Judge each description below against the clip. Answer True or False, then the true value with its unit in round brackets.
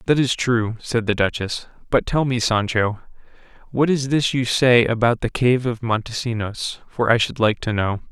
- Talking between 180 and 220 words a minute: True (190 wpm)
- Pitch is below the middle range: True (120 Hz)